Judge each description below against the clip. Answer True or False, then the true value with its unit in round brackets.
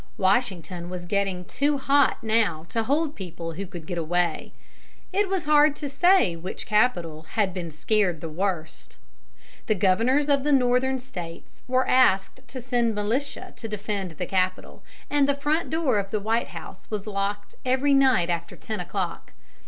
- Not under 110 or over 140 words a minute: False (170 wpm)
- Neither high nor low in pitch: False (210 Hz)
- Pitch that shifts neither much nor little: False (6.6 semitones)